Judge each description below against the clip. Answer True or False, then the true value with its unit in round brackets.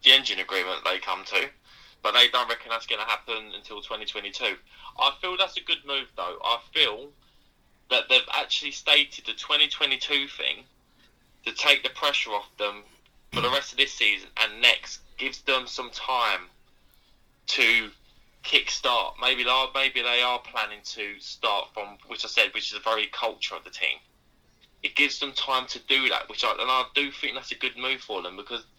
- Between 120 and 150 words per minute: False (190 wpm)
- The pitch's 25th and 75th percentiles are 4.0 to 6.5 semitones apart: False (3.2 semitones)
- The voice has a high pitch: False (130 Hz)